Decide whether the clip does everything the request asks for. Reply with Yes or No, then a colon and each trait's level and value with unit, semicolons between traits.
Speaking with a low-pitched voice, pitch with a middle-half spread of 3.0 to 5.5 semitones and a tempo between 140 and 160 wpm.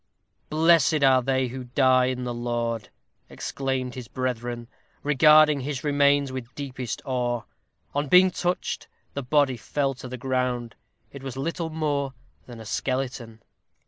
No: low, 130 Hz; narrow, 2.6 semitones; average, 145 wpm